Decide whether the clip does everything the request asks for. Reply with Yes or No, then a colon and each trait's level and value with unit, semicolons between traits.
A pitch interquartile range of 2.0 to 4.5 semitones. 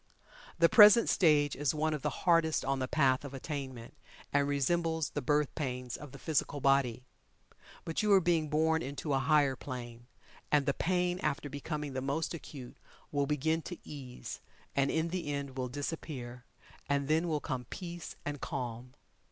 Yes: average, 3.3 semitones